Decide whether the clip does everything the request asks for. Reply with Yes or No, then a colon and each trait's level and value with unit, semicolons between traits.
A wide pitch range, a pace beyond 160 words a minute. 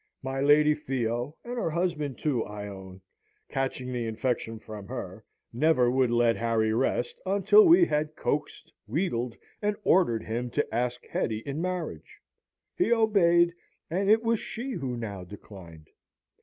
No: wide, 7.1 semitones; average, 150 wpm